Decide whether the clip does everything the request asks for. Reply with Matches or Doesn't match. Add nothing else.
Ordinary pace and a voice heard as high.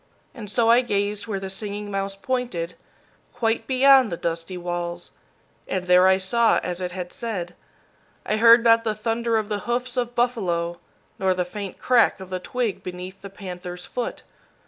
Matches